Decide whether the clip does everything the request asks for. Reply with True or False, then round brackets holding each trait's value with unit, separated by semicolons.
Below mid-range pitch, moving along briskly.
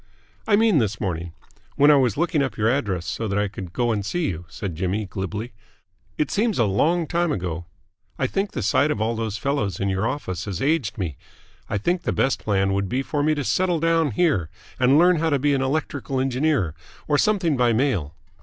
True (125 Hz; 220 wpm)